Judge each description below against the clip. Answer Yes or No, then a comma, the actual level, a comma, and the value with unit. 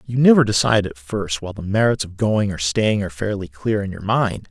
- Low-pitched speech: Yes, low, 100 Hz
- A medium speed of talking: No, fast, 240 wpm